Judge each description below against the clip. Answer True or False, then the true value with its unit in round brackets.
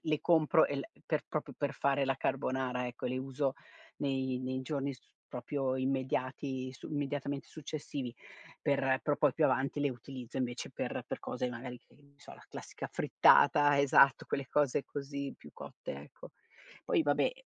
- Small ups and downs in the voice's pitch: True (1.8 semitones)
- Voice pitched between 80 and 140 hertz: True (135 Hz)